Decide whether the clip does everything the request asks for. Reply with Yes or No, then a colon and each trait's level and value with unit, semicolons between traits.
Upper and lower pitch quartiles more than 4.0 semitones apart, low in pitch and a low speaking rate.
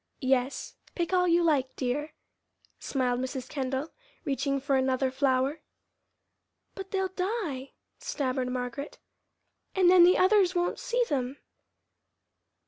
No: wide, 5.4 semitones; very high, 280 Hz; slow, 120 wpm